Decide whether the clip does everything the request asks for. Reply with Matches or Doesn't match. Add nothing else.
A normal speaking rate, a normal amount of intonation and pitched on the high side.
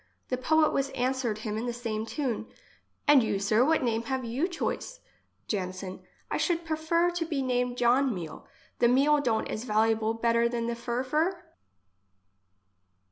Matches